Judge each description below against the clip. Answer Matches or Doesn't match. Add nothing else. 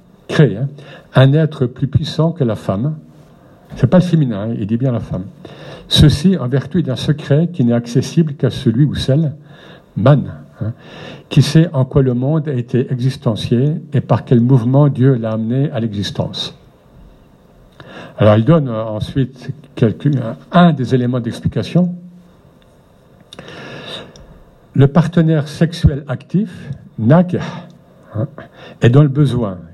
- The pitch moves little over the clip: Doesn't match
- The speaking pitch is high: Doesn't match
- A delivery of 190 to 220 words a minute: Doesn't match